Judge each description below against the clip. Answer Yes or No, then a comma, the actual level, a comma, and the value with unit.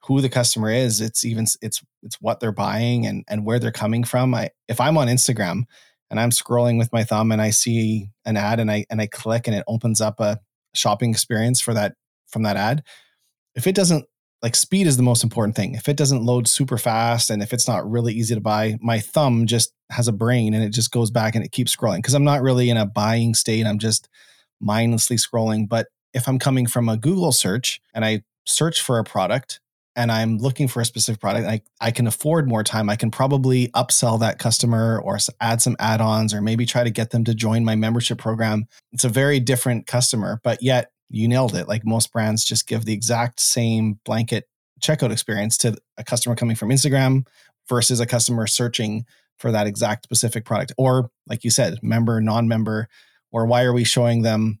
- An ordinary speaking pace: No, fast, 220 wpm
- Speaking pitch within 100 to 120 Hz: Yes, low, 115 Hz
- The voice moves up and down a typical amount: No, narrow, 1.9 semitones